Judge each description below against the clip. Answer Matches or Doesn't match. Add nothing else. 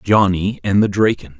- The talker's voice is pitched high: Doesn't match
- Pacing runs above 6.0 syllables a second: Doesn't match